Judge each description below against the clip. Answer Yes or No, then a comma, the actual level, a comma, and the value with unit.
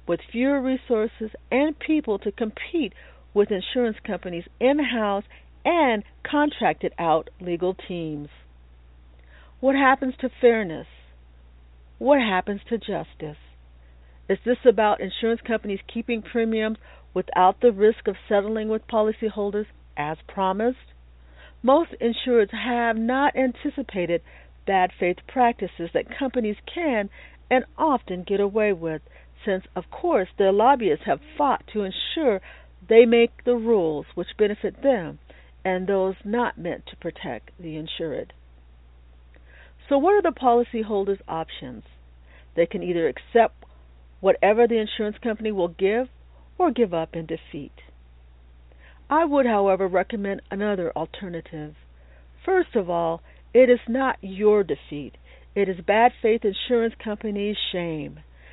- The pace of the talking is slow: Yes, slow, 125 wpm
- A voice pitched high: Yes, high, 205 Hz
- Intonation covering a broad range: Yes, wide, 6.7 semitones